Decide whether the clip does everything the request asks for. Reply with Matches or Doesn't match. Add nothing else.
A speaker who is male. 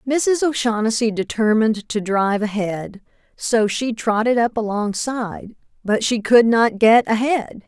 Doesn't match